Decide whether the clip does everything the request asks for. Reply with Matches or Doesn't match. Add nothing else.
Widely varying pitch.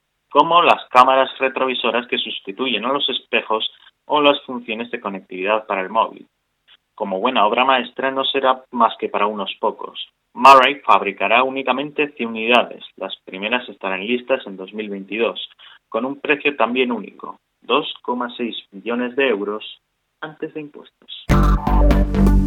Doesn't match